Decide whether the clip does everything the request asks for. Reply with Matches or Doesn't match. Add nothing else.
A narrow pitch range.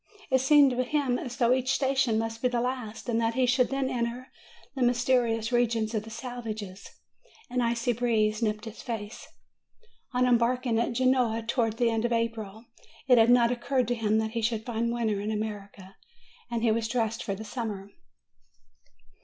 Matches